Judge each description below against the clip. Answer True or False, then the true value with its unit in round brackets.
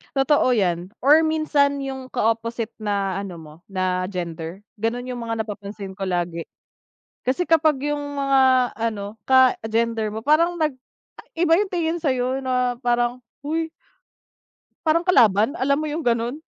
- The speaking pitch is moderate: False (245 Hz)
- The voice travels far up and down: True (5.7 semitones)